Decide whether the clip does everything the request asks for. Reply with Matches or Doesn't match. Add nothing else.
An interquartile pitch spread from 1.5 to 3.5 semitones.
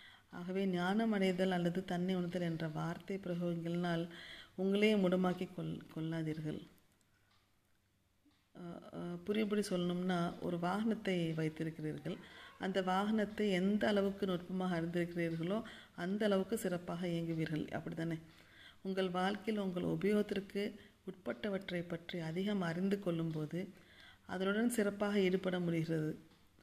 Matches